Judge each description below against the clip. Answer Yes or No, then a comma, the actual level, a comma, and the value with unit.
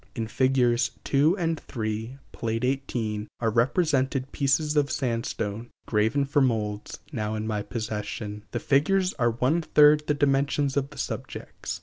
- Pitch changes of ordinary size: Yes, average, 4.3 semitones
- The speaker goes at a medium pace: Yes, average, 150 wpm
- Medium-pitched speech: No, low, 130 Hz